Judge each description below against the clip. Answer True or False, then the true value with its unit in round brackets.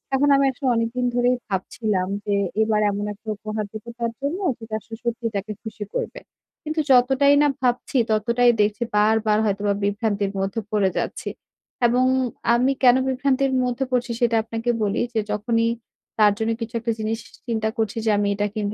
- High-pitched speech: True (225 Hz)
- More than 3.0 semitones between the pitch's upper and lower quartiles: False (2.7 semitones)